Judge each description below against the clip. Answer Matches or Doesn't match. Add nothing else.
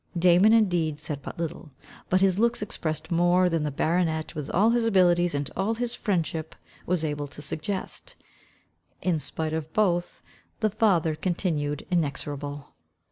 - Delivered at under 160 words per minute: Matches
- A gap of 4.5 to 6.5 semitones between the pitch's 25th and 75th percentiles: Doesn't match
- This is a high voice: Doesn't match